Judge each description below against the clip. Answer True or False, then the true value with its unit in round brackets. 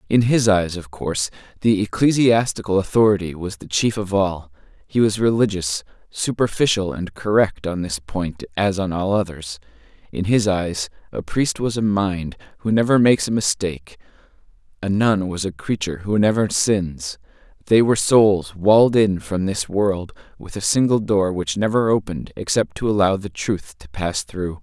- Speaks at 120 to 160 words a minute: False (170 wpm)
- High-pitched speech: False (100 Hz)